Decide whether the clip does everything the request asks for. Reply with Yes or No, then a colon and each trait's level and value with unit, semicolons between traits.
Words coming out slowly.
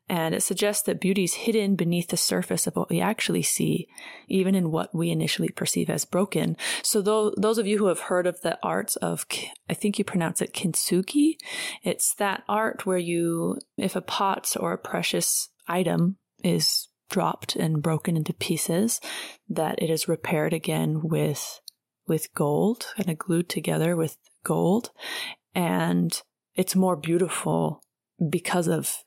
No: average, 165 wpm